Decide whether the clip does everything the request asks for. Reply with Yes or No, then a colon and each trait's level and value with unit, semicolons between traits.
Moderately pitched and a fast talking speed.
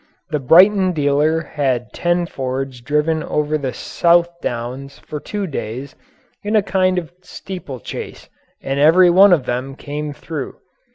No: medium, 150 Hz; average, 140 wpm